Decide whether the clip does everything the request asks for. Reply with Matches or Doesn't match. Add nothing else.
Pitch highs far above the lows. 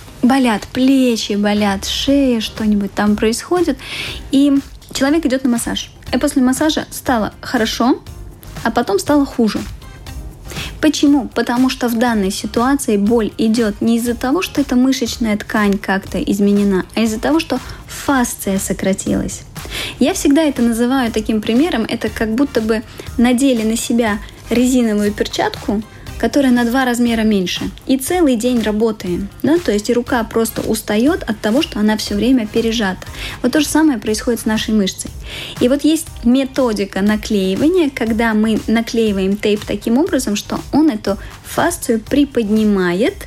Doesn't match